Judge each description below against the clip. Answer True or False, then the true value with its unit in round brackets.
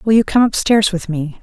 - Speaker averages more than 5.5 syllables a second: False (5.3 syllables/s)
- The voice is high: True (200 Hz)